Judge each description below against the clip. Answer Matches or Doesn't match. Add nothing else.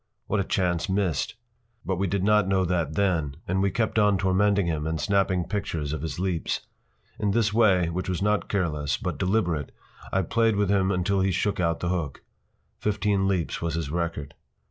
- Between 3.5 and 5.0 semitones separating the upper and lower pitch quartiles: Doesn't match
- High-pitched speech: Doesn't match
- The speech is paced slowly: Doesn't match